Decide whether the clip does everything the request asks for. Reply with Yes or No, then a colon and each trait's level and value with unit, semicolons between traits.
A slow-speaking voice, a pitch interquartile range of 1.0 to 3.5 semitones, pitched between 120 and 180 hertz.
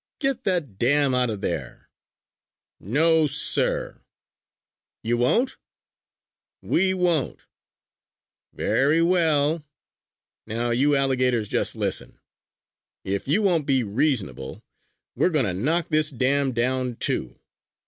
No: slow, 110 wpm; average, 5.2 semitones; medium, 140 Hz